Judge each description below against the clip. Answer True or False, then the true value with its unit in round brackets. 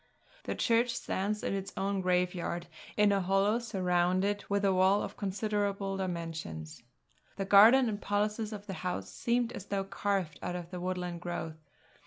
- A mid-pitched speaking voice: False (195 Hz)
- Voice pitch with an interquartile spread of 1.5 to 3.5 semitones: True (2.4 semitones)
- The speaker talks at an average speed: True (165 wpm)